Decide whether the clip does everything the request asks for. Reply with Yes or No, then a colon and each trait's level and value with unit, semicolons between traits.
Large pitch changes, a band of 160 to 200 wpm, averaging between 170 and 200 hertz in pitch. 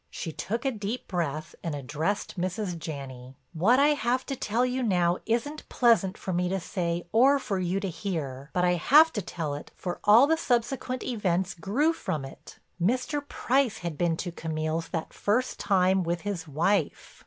Yes: wide, 6.2 semitones; average, 180 wpm; high, 190 Hz